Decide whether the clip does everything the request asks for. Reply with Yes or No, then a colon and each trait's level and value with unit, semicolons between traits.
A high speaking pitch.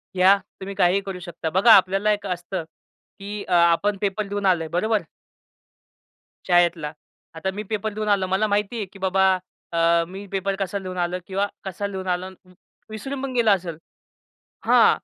Yes: high, 195 Hz